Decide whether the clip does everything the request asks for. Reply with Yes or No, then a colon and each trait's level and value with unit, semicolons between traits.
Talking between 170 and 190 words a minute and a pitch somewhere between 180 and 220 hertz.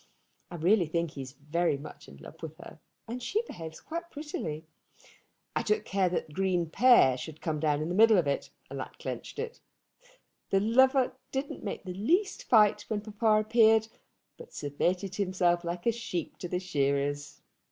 Yes: average, 180 wpm; medium, 185 Hz